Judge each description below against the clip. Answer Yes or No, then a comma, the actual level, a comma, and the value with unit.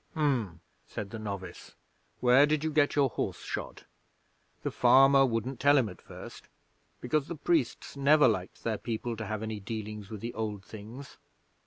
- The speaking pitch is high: No, low, 115 Hz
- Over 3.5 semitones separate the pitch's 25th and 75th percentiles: Yes, average, 4.6 semitones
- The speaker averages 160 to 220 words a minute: Yes, average, 170 wpm